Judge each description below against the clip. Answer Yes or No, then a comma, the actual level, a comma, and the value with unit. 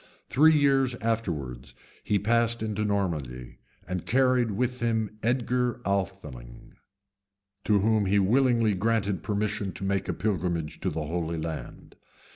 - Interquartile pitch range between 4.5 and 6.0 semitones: Yes, average, 4.9 semitones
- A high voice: No, low, 105 Hz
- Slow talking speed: Yes, slow, 130 wpm